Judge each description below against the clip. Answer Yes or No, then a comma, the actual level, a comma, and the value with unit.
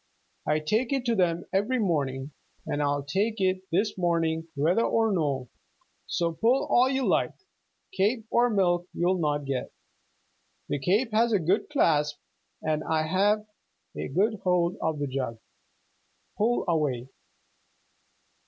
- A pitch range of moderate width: No, wide, 6.2 semitones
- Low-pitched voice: No, medium, 175 Hz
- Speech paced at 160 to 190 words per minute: No, average, 140 wpm